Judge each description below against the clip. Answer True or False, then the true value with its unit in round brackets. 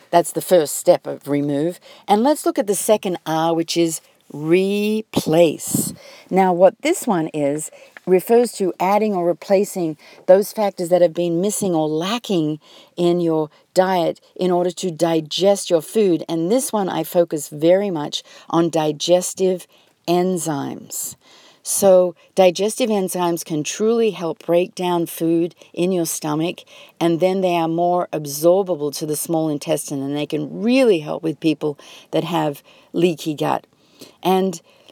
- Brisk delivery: False (150 wpm)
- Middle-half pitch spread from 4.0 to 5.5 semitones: False (2.9 semitones)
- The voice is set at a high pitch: False (175 Hz)